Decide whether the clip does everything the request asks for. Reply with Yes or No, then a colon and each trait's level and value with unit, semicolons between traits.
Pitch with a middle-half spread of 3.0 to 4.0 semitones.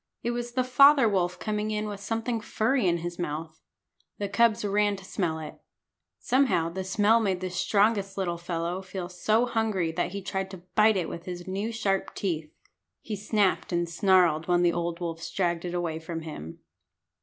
Yes: average, 3.7 semitones